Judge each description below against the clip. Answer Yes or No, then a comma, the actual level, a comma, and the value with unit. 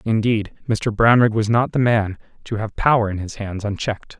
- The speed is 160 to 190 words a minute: No, average, 200 wpm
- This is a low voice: Yes, low, 110 Hz